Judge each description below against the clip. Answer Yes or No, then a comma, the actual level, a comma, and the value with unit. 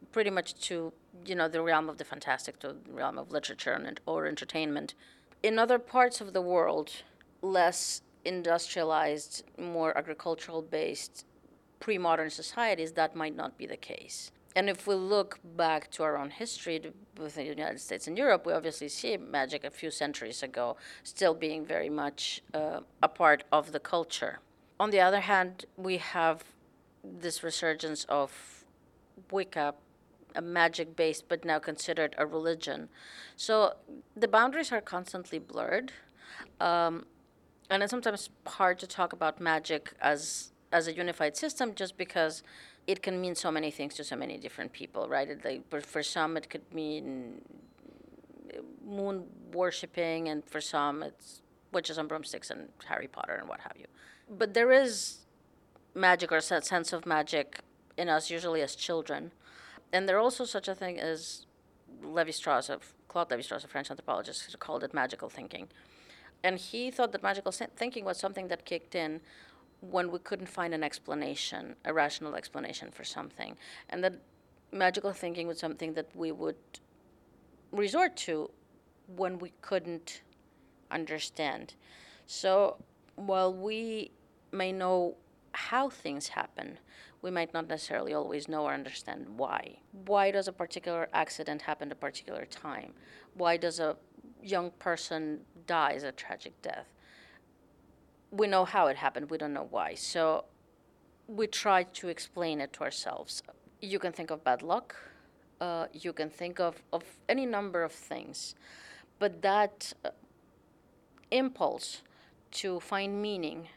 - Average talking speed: Yes, average, 155 wpm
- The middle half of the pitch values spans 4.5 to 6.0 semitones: No, average, 3.4 semitones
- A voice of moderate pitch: Yes, medium, 170 Hz